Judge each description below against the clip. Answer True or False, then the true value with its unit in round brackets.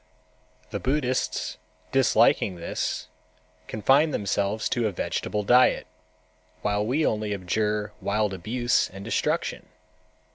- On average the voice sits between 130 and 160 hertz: False (105 Hz)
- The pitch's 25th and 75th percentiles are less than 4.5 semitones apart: True (3.6 semitones)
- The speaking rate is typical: False (105 wpm)